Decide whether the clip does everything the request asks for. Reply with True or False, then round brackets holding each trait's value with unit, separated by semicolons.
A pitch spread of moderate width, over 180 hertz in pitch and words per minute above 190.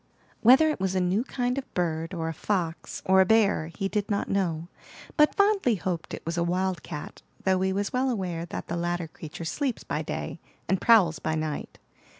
True (4.6 semitones; 190 Hz; 200 wpm)